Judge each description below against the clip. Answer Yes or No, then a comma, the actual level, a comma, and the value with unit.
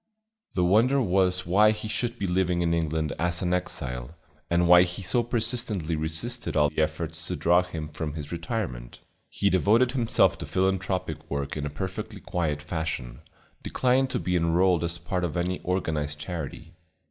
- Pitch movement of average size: Yes, average, 3.3 semitones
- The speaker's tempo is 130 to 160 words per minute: No, average, 170 wpm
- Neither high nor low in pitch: No, very low, 90 Hz